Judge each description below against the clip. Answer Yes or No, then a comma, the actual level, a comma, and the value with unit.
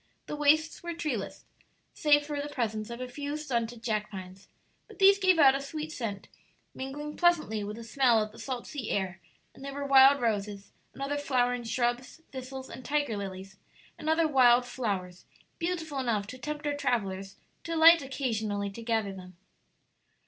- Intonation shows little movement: No, wide, 5.4 semitones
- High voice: Yes, very high, 255 Hz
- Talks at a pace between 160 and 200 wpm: Yes, average, 180 wpm